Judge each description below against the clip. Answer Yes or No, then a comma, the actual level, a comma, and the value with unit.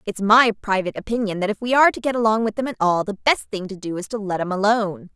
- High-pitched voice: Yes, high, 210 Hz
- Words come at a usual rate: No, fast, 290 wpm